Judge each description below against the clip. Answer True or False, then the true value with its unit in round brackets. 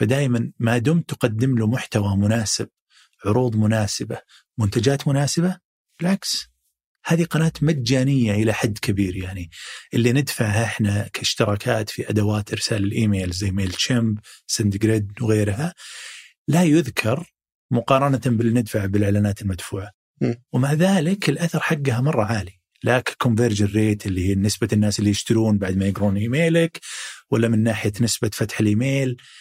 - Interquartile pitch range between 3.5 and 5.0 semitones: True (4.5 semitones)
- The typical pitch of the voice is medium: False (115 Hz)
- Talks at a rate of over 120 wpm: True (130 wpm)